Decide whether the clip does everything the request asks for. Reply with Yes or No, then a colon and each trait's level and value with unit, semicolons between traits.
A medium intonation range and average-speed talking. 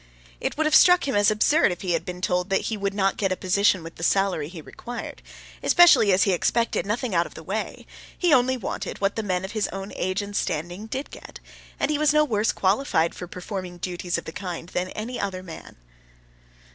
No: average, 3.8 semitones; fast, 225 wpm